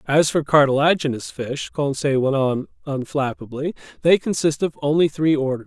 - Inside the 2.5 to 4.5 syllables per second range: No, 5.1 syllables/s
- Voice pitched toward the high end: No, medium, 145 Hz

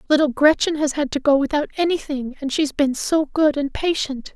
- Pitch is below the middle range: No, very high, 290 Hz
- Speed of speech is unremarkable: No, fast, 220 wpm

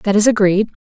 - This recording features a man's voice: No, female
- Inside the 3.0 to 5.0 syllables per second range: No, 5.8 syllables/s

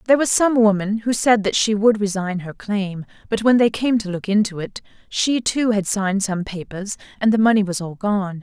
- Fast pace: Yes, fast, 230 wpm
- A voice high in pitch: Yes, high, 205 Hz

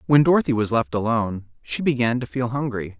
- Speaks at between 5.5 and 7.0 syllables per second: Yes, 5.9 syllables/s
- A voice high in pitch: No, low, 120 Hz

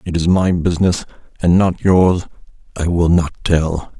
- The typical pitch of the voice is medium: No, very low, 85 Hz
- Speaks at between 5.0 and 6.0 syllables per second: No, 4.7 syllables/s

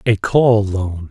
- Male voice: Yes, male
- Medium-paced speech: Yes, average, 160 wpm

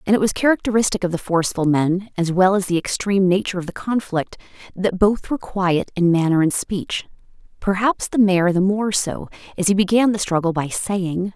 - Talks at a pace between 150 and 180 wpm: No, average, 195 wpm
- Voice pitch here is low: No, high, 190 Hz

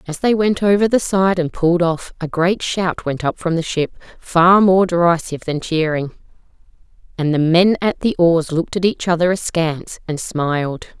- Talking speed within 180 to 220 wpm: Yes, average, 190 wpm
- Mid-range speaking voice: Yes, medium, 175 Hz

